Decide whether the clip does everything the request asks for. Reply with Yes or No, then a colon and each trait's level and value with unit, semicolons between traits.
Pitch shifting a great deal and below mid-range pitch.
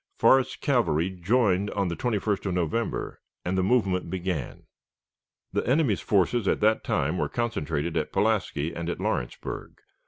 No: average, 5.0 semitones; very low, 95 Hz